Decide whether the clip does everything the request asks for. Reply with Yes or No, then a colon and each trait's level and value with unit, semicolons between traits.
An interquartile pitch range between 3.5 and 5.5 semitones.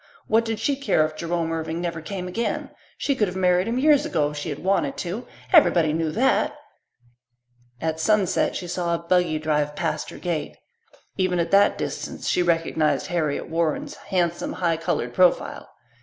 No: average, 3.1 semitones